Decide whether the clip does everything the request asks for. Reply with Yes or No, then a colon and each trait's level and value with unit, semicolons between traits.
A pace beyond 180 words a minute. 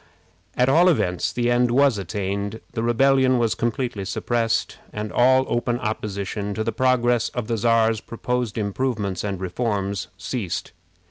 No: average, 145 wpm